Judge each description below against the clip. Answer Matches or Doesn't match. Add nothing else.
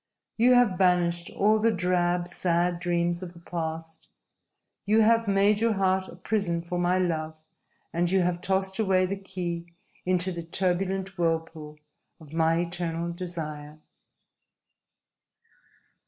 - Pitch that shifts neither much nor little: Doesn't match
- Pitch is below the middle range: Doesn't match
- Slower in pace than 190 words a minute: Matches